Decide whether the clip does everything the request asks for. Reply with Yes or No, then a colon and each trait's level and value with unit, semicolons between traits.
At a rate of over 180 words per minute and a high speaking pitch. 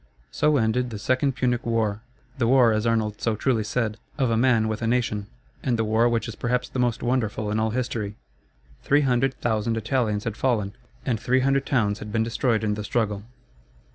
No: average, 200 wpm; low, 115 Hz